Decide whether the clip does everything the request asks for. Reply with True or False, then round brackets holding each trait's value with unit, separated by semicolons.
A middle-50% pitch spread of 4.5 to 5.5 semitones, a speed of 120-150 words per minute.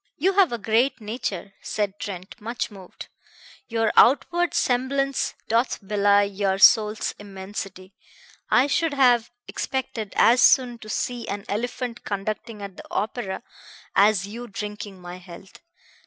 False (3.5 semitones; 135 wpm)